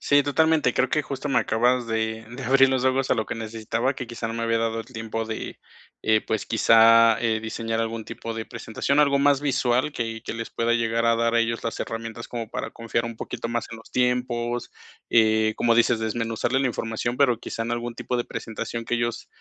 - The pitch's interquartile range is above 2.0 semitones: No, narrow, 1.6 semitones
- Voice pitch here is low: Yes, low, 115 Hz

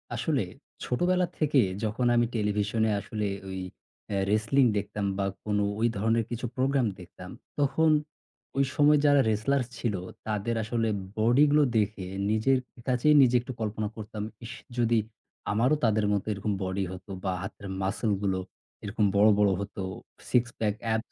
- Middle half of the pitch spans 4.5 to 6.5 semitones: No, average, 3.2 semitones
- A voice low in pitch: Yes, low, 110 Hz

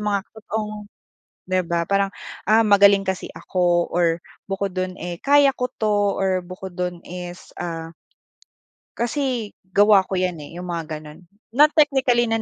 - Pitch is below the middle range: No, high, 195 Hz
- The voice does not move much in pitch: No, average, 3.6 semitones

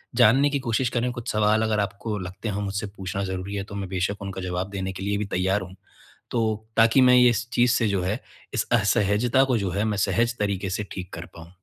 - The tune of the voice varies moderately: Yes, average, 3.3 semitones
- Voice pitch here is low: Yes, low, 105 Hz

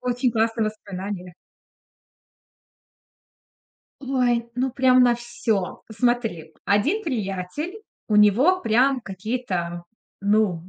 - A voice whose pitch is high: Yes, high, 225 Hz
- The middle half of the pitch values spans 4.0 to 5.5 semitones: Yes, average, 4.3 semitones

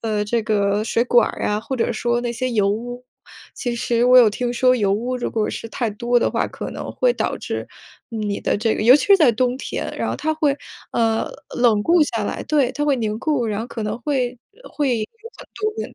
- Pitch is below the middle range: No, high, 240 Hz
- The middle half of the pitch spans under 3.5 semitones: Yes, average, 2.7 semitones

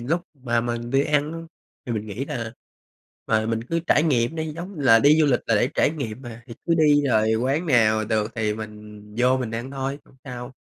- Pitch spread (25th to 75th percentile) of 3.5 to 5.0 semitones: Yes, average, 4.4 semitones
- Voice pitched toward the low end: Yes, low, 125 Hz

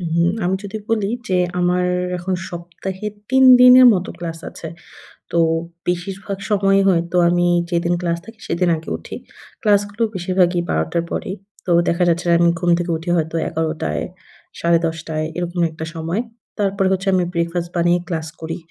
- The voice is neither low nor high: Yes, medium, 175 Hz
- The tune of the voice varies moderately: No, narrow, 2.2 semitones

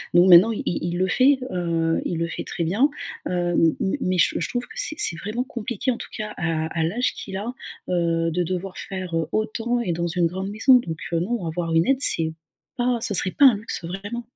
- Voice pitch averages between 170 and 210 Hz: Yes, medium, 185 Hz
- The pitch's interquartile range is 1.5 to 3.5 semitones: No, wide, 5.7 semitones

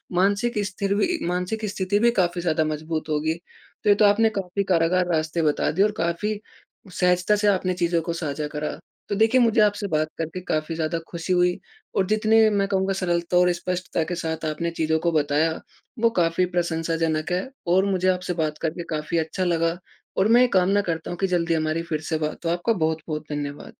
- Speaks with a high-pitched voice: No, medium, 175 Hz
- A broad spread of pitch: No, average, 3.4 semitones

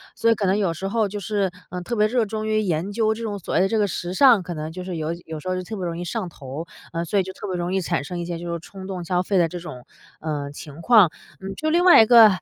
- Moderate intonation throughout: Yes, average, 4.0 semitones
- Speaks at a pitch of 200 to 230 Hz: No, medium, 185 Hz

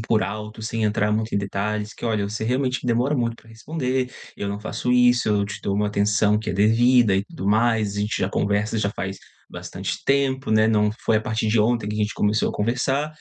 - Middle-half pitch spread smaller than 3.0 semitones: Yes, narrow, 2.5 semitones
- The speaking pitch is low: Yes, low, 110 Hz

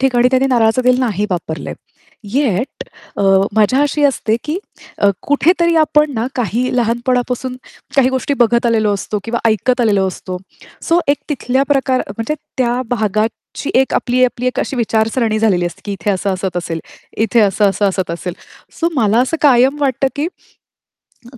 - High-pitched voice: Yes, high, 240 Hz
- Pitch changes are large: No, average, 3.9 semitones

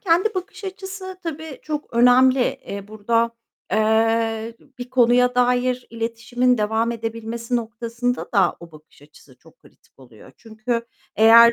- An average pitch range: No, narrow, 2.2 semitones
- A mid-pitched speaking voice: No, high, 235 Hz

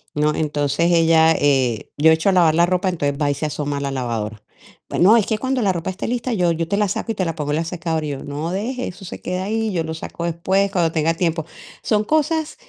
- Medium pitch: Yes, medium, 165 Hz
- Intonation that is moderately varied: Yes, average, 4.5 semitones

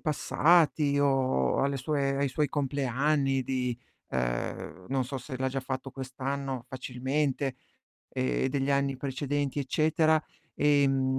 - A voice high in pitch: No, low, 135 Hz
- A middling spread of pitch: No, narrow, 1.6 semitones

